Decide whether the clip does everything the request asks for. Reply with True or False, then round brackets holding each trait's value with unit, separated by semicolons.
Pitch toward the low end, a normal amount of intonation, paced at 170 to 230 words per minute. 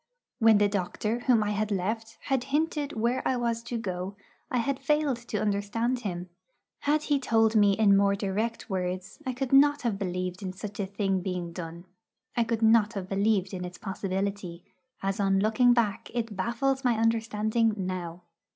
False (215 Hz; 3.5 semitones; 180 wpm)